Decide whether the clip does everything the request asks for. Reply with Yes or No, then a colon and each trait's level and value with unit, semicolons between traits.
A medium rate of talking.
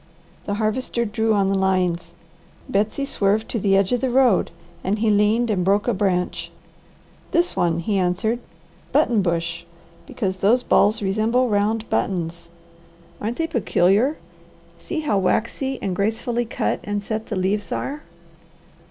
Yes: average, 145 wpm